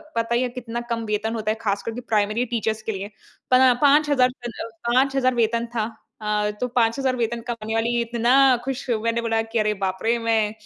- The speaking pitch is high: Yes, high, 230 Hz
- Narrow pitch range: Yes, narrow, 2.3 semitones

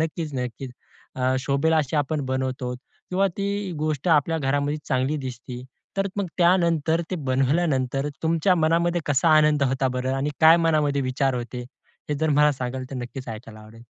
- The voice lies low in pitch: No, medium, 145 Hz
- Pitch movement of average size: Yes, average, 3.7 semitones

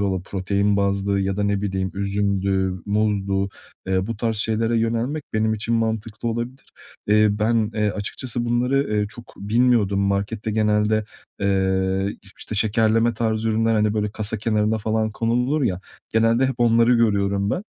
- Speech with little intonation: Yes, narrow, 2.3 semitones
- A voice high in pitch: No, low, 105 Hz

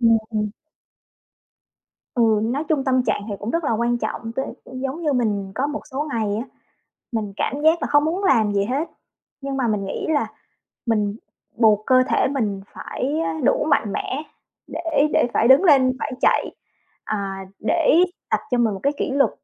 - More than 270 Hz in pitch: No, very high, 255 Hz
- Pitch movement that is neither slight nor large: Yes, average, 5.0 semitones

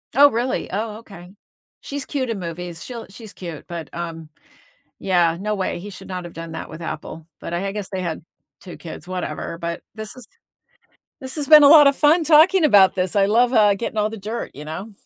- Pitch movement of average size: No, wide, 5.7 semitones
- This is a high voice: Yes, high, 200 Hz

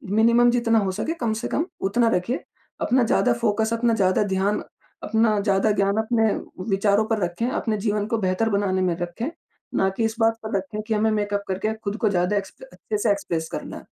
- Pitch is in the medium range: No, high, 215 Hz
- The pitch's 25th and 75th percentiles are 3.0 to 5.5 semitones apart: No, narrow, 2.4 semitones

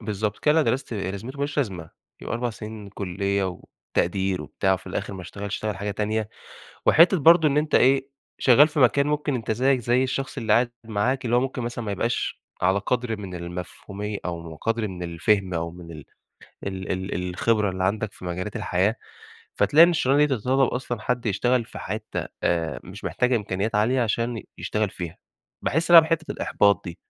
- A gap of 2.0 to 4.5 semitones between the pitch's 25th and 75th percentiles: No, average, 5.0 semitones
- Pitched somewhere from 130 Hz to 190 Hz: No, low, 110 Hz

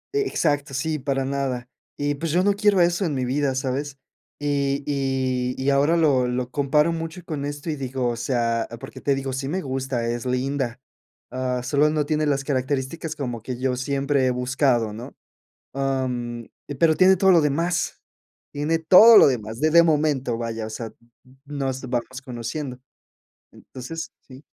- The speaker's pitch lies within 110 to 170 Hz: Yes, low, 135 Hz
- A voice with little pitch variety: No, average, 3.0 semitones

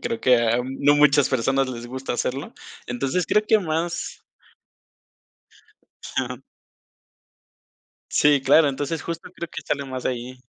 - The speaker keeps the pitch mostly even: No, average, 3.4 semitones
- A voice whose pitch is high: No, low, 135 Hz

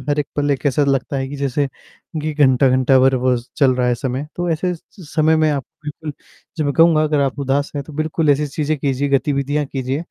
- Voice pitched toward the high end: No, medium, 145 Hz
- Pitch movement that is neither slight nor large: No, narrow, 2.3 semitones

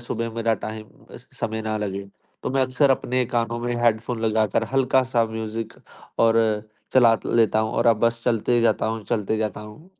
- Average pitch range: No, narrow, 1.7 semitones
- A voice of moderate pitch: No, low, 115 Hz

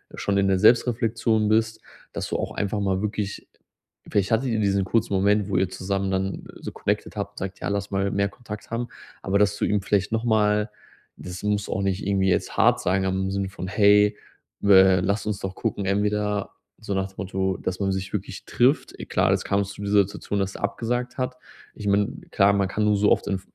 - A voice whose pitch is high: No, low, 100 Hz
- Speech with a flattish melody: Yes, narrow, 1.5 semitones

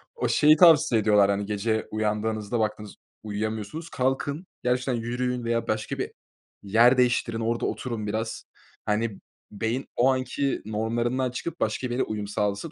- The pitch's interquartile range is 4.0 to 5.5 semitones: No, average, 3.0 semitones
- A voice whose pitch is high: No, low, 115 Hz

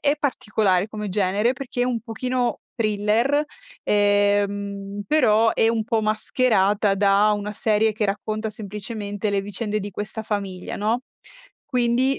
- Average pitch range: No, narrow, 2.2 semitones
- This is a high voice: Yes, high, 210 Hz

